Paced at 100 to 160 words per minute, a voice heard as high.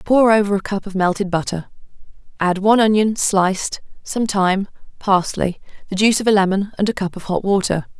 No: average, 190 wpm; high, 200 Hz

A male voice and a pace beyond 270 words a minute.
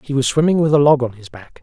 Yes: male; fast, 330 wpm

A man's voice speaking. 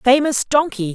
No: female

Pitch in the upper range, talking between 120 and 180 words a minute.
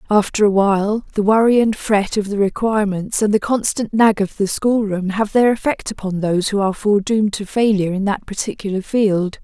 No: high, 205 Hz; average, 195 wpm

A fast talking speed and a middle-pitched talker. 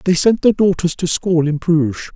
Yes: fast, 225 wpm; medium, 175 Hz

